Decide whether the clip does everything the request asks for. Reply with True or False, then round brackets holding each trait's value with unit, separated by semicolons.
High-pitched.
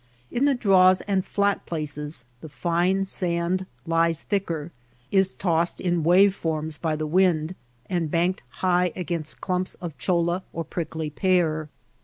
False (175 Hz)